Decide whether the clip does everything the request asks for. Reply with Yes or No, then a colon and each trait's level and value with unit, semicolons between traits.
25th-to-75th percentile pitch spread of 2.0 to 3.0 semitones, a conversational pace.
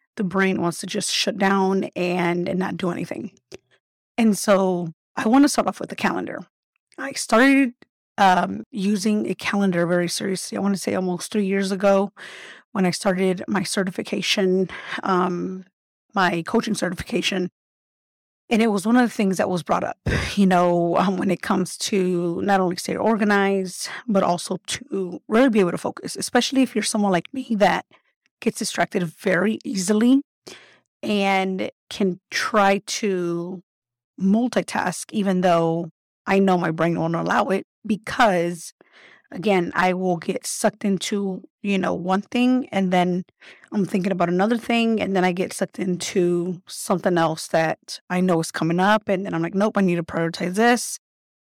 Yes: average, 2.7 semitones; average, 170 wpm